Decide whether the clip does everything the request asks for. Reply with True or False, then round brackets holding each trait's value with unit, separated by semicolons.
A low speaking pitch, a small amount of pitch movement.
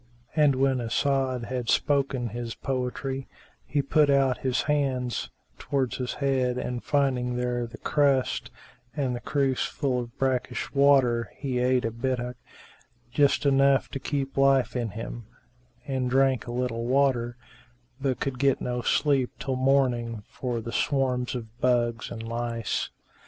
True (130 Hz; 2.0 semitones)